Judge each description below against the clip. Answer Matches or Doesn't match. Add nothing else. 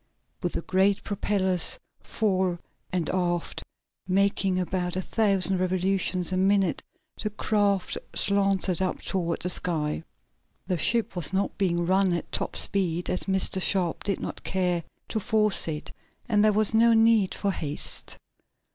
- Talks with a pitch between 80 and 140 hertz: Doesn't match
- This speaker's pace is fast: Doesn't match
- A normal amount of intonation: Doesn't match